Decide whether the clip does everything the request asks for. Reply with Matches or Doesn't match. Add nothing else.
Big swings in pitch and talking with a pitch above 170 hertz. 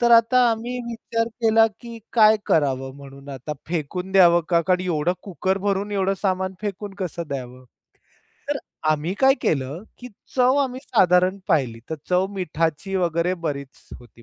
Matches